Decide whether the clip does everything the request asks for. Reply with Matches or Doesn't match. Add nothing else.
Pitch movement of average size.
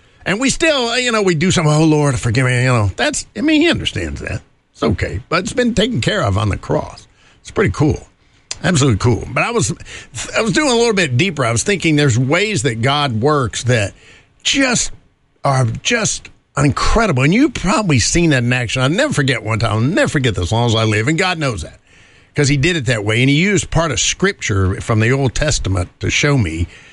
Doesn't match